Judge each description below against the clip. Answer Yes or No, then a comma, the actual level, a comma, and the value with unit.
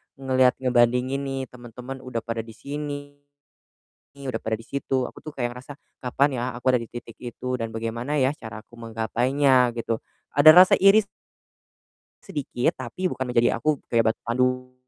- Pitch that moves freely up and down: No, narrow, 2.6 semitones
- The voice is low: Yes, low, 125 Hz